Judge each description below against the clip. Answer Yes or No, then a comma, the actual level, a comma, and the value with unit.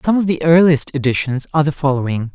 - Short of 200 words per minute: No, fast, 205 wpm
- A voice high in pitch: No, medium, 145 Hz